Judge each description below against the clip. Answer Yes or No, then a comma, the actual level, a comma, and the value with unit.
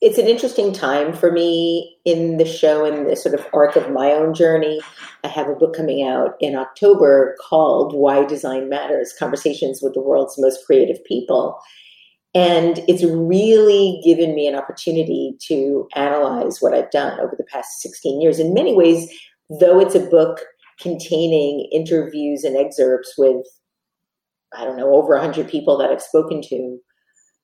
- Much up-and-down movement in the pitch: No, average, 3.0 semitones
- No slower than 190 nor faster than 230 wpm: No, average, 165 wpm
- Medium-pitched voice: Yes, medium, 160 Hz